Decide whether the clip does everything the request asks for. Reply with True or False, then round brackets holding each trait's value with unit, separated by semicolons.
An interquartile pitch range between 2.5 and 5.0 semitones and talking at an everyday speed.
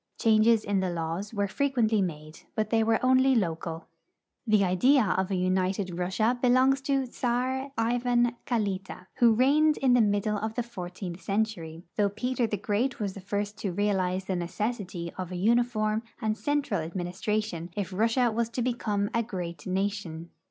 True (4.4 semitones; 170 wpm)